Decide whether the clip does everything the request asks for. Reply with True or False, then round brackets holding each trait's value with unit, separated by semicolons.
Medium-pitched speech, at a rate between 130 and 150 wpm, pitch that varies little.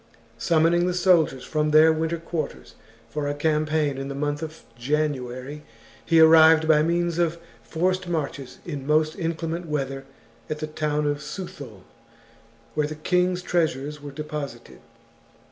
True (155 Hz; 145 wpm; 2.2 semitones)